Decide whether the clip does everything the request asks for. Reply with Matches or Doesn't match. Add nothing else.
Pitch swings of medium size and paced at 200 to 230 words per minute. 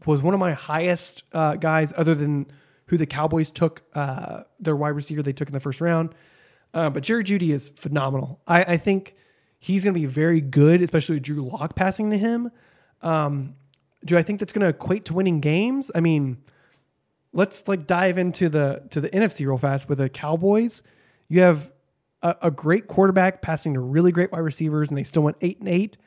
Matches